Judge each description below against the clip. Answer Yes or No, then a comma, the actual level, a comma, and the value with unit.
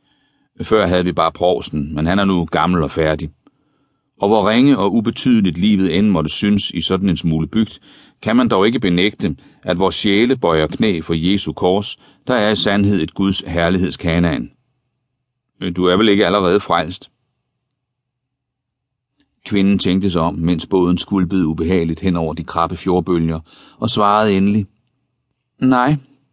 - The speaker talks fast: No, average, 155 wpm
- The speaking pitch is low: Yes, very low, 95 Hz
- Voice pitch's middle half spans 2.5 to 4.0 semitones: No, average, 4.6 semitones